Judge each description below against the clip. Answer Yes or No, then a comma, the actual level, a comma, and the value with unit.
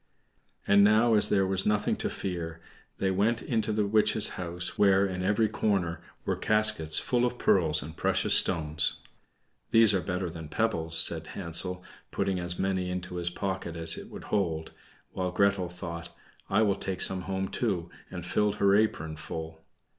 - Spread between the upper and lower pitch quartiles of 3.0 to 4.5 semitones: Yes, average, 3.4 semitones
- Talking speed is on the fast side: No, average, 170 wpm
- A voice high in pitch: No, very low, 95 Hz